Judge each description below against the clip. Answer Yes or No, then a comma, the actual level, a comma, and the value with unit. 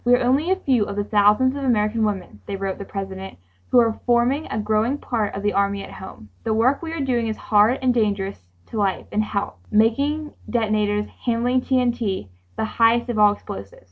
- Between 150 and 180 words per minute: No, fast, 205 wpm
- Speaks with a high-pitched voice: Yes, high, 220 Hz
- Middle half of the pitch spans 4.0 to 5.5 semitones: No, average, 3.3 semitones